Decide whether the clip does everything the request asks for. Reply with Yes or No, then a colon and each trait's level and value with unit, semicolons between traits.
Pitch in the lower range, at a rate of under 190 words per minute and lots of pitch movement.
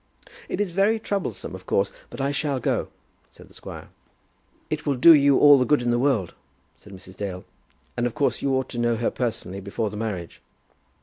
No: low, 120 Hz; fast, 205 wpm; wide, 5.9 semitones